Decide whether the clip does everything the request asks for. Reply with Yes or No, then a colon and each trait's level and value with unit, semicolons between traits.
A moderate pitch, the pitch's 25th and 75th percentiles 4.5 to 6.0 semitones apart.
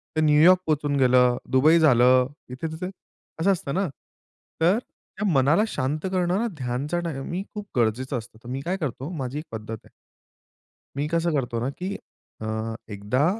Yes: medium, 145 Hz; average, 5.2 semitones